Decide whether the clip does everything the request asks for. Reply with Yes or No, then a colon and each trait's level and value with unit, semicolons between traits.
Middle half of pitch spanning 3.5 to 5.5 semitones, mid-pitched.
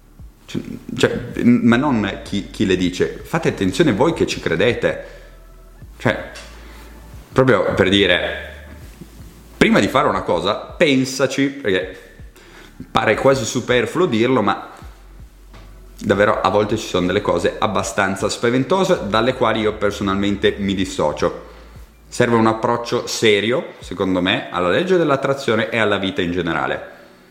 No: average, 4.5 semitones; low, 105 Hz